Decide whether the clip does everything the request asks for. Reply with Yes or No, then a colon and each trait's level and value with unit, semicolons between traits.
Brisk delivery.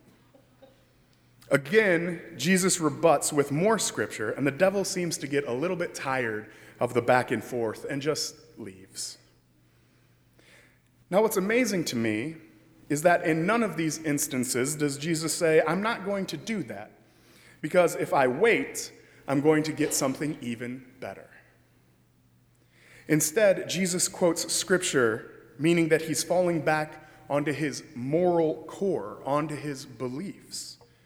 No: average, 140 wpm